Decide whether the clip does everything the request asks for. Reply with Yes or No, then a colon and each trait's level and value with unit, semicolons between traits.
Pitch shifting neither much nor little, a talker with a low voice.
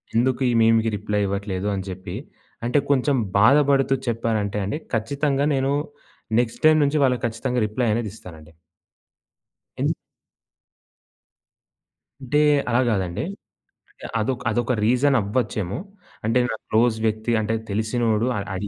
Yes: average, 3.6 semitones; low, 115 Hz